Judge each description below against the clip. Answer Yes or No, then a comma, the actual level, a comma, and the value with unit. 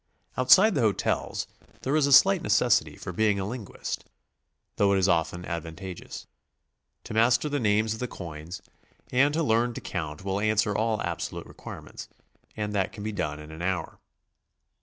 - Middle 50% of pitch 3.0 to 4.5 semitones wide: No, average, 5.2 semitones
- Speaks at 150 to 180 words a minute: Yes, average, 170 wpm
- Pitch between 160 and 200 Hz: No, low, 105 Hz